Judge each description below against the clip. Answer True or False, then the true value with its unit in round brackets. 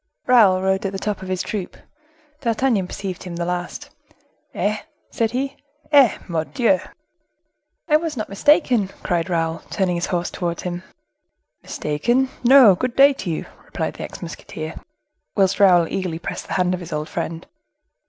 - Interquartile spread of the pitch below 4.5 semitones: False (5.5 semitones)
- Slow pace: False (160 wpm)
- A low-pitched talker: False (190 Hz)